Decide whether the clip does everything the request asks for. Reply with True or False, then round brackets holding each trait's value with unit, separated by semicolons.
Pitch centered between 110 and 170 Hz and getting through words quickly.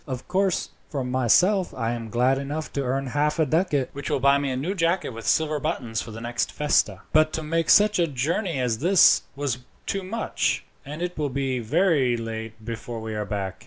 True (140 Hz; 210 wpm)